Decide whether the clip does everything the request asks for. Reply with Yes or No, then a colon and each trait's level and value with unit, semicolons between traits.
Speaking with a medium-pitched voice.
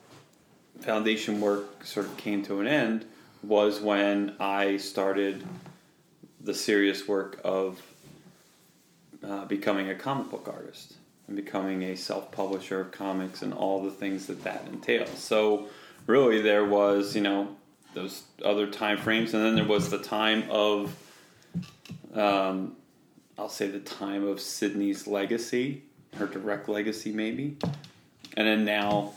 No: low, 105 Hz